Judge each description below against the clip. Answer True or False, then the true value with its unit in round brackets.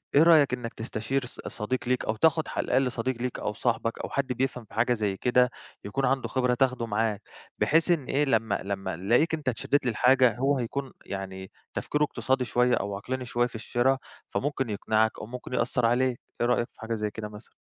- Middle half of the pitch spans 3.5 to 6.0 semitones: False (3.0 semitones)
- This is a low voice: True (125 Hz)